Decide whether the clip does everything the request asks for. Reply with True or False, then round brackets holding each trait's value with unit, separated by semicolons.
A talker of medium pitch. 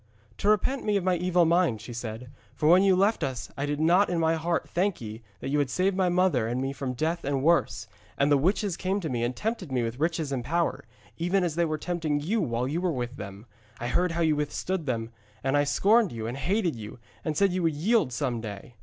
True (155 Hz)